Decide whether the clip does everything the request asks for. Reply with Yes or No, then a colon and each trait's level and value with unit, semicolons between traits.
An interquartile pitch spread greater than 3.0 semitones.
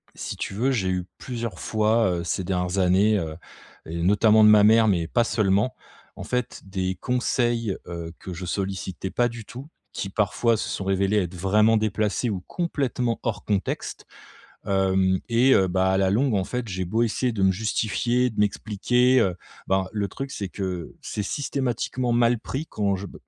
Yes: average, 3.7 semitones